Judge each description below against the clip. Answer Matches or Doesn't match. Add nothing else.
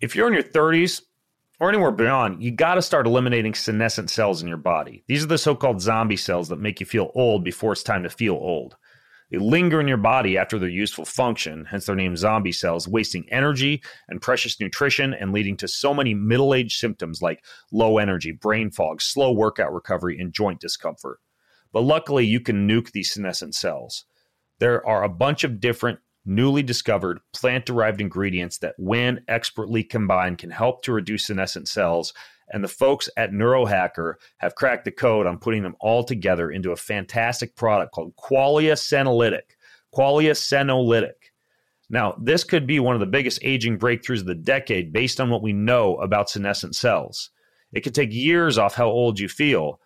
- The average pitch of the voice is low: Matches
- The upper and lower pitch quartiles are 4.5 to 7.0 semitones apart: Matches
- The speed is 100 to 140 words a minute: Doesn't match